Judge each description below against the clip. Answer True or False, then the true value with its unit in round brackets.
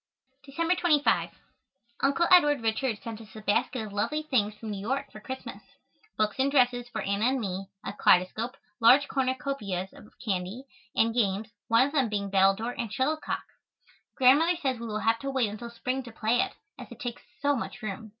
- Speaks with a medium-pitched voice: False (235 Hz)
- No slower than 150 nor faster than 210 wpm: True (190 wpm)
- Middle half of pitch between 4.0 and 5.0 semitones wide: True (4.3 semitones)